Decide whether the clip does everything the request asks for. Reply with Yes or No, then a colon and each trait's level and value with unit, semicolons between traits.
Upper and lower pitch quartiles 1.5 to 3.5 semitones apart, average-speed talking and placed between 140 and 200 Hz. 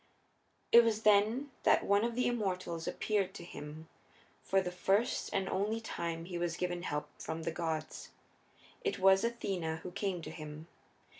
No: average, 4.2 semitones; average, 165 wpm; medium, 185 Hz